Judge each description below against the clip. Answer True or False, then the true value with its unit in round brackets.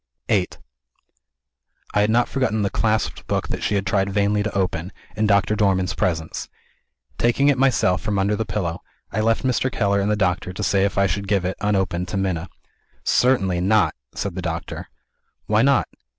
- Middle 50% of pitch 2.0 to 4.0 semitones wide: True (2.4 semitones)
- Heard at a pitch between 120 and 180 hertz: False (100 Hz)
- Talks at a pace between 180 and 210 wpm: True (185 wpm)